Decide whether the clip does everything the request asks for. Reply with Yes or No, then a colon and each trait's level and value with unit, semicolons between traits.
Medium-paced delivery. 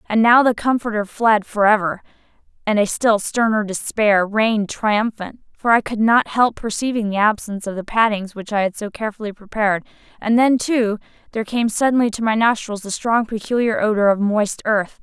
Yes: average, 185 wpm